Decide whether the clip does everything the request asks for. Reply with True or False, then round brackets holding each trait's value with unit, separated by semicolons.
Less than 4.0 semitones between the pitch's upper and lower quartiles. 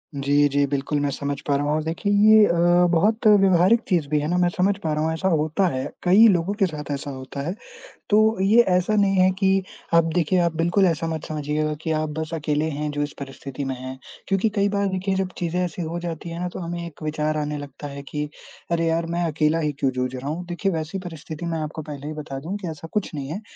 True (3.6 semitones)